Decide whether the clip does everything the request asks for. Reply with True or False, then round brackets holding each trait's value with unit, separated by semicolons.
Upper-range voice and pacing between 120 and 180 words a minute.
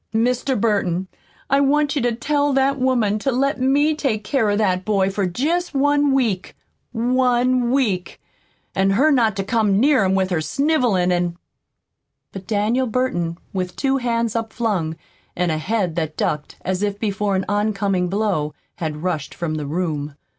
True (215 Hz; 170 wpm)